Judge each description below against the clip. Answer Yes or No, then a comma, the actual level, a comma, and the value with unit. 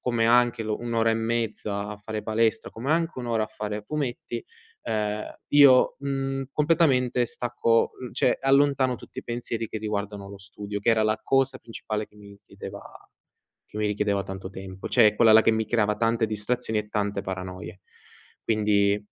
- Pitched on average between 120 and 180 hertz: No, low, 110 Hz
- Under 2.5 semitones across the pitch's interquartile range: No, average, 2.8 semitones